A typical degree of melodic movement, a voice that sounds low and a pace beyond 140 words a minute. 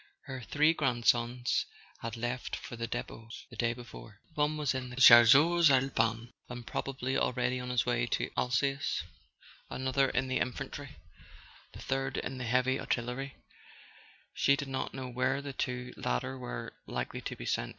No: narrow, 2.0 semitones; low, 125 Hz; average, 170 wpm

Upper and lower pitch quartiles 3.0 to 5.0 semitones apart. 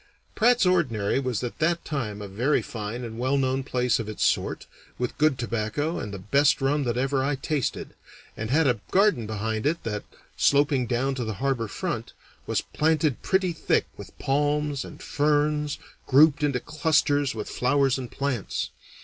Yes: average, 4.0 semitones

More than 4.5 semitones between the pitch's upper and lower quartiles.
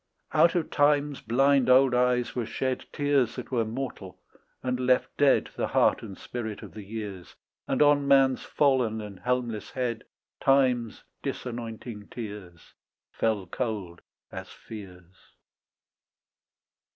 No: average, 3.8 semitones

